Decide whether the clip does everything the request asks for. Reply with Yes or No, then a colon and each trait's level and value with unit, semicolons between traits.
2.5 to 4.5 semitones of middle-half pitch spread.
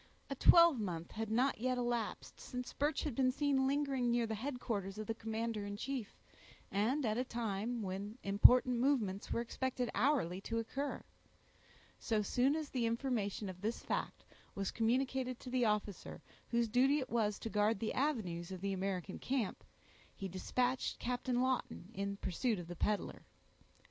Yes: average, 4.0 semitones